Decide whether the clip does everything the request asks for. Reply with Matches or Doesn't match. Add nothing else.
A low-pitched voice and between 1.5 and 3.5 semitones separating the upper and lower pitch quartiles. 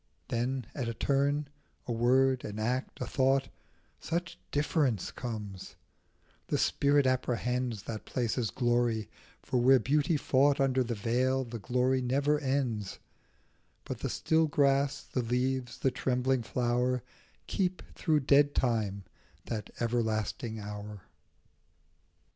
Matches